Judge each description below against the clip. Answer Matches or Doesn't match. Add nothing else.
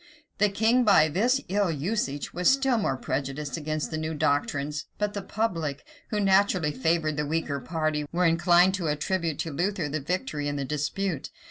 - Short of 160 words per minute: Doesn't match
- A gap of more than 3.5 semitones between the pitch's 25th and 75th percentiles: Matches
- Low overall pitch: Doesn't match